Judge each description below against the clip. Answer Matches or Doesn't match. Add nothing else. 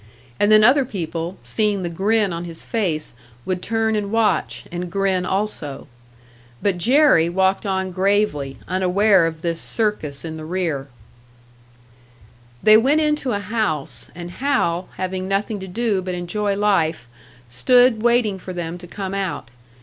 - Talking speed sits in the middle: Matches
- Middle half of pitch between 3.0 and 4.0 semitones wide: Matches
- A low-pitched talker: Doesn't match